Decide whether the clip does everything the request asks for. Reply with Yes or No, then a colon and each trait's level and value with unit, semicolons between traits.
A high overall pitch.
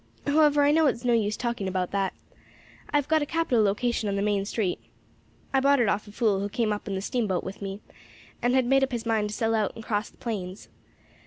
Yes: high, 225 Hz